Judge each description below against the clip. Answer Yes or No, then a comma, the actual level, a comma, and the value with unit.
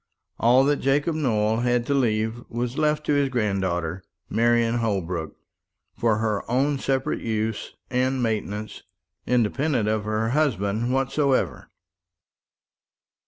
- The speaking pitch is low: Yes, low, 120 Hz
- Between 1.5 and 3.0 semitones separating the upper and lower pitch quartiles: No, average, 3.8 semitones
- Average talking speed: No, slow, 115 wpm